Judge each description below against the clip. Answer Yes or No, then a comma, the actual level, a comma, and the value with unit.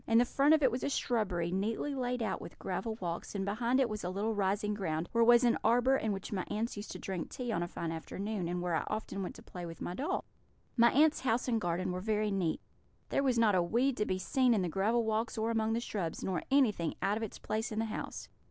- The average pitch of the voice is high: Yes, high, 215 Hz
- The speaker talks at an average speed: No, fast, 265 wpm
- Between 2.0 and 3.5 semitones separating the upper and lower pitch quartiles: No, average, 4.1 semitones